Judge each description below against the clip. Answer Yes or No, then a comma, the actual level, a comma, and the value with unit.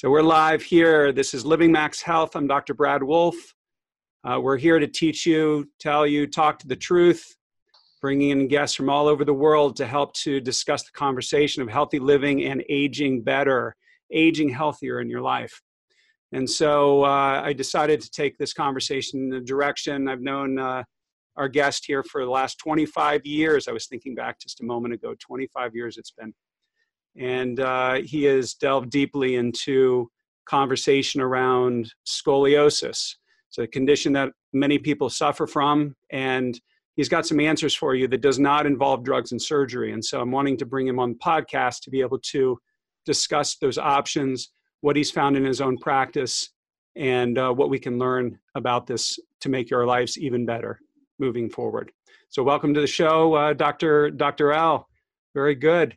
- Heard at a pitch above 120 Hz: Yes, medium, 140 Hz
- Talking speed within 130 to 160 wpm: No, average, 180 wpm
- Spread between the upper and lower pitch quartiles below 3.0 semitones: Yes, narrow, 2.4 semitones